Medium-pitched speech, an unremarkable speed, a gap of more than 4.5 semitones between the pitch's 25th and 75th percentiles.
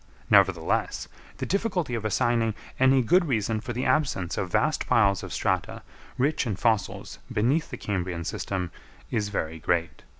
No: low, 110 Hz; average, 155 wpm; wide, 5.6 semitones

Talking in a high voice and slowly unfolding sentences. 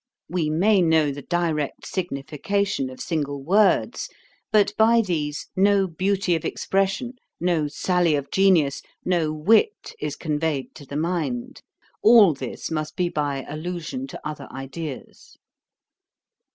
No: medium, 165 Hz; slow, 130 wpm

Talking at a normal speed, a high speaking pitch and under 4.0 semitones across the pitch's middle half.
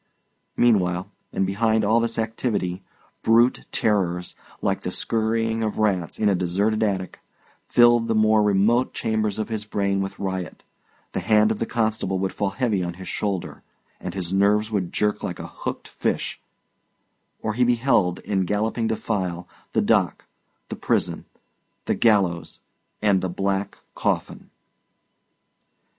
No: average, 145 wpm; low, 105 Hz; average, 2.7 semitones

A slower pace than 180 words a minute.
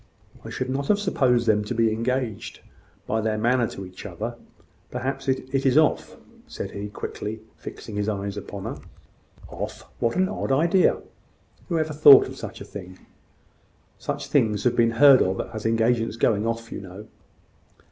Yes: average, 170 wpm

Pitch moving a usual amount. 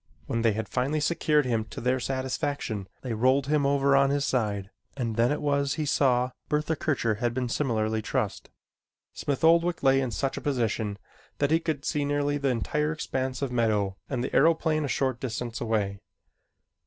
Yes: average, 3.8 semitones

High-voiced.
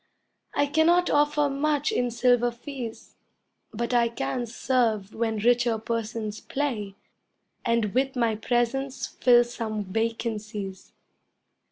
Yes: high, 235 Hz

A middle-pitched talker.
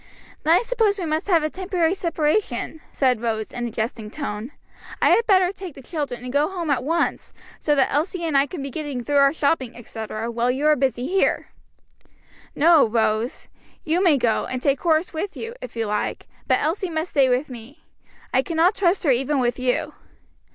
No: very high, 290 Hz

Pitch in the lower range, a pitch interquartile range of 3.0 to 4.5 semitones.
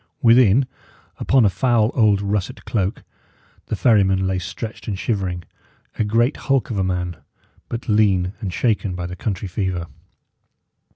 Yes: low, 100 Hz; average, 3.5 semitones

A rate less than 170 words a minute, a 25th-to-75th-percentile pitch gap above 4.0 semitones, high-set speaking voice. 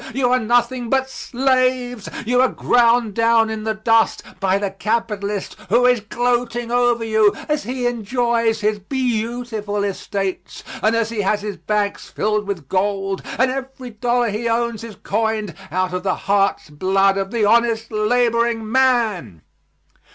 No: average, 155 wpm; average, 2.9 semitones; high, 225 Hz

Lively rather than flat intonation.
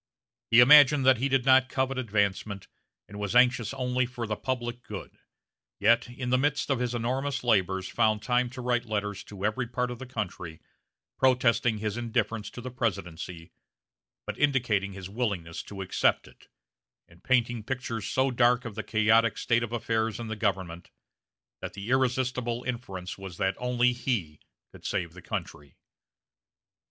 No: average, 3.6 semitones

